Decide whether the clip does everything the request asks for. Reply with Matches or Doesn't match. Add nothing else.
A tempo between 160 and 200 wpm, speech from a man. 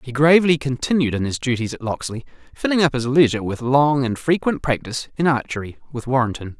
Matches